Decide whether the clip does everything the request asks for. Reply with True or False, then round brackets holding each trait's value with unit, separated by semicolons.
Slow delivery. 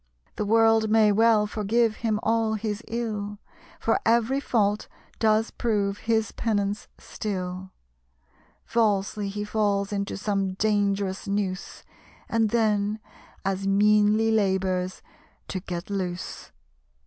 True (115 wpm)